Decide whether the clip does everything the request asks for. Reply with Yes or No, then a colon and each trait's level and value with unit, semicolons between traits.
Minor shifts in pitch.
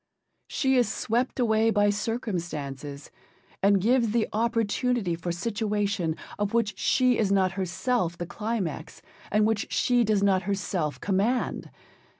No: average, 3.7 semitones